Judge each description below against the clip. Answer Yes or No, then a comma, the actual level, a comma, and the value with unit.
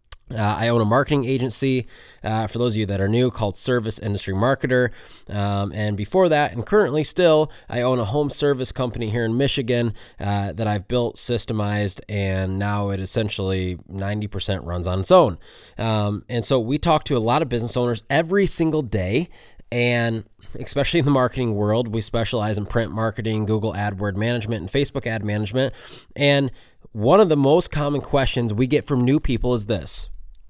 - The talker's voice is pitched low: Yes, low, 115 Hz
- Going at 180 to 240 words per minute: Yes, average, 185 wpm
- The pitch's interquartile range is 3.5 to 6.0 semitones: Yes, average, 4.2 semitones